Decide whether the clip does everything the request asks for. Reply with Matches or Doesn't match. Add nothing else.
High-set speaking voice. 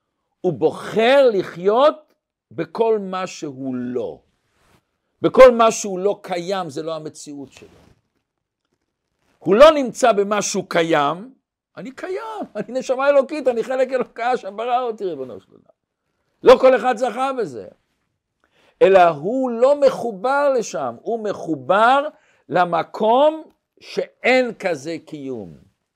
Matches